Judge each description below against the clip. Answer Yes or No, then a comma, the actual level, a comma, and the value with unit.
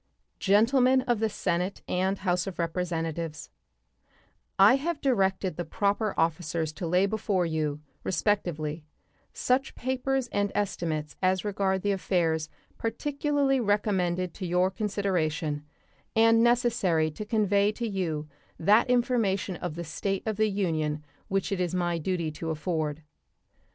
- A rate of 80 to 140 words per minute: Yes, slow, 135 wpm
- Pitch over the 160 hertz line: Yes, high, 190 Hz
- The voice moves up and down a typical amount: Yes, average, 4.4 semitones